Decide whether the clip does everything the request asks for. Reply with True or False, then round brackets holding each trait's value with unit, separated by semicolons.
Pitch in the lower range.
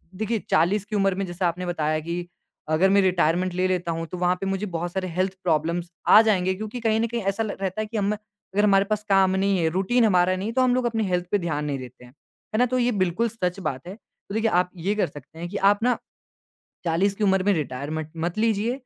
False (190 Hz)